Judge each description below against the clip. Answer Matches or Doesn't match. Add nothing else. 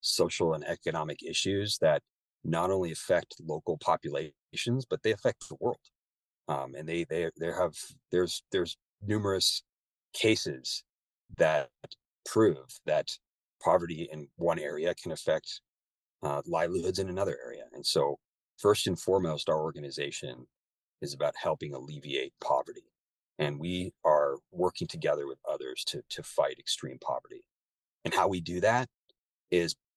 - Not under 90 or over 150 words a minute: Matches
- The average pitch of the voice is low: Matches